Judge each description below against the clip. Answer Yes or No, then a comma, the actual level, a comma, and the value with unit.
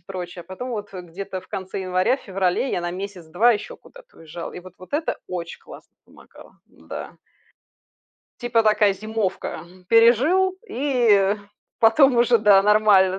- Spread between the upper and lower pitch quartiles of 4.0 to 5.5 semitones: Yes, average, 4.3 semitones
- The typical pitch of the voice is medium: No, high, 205 Hz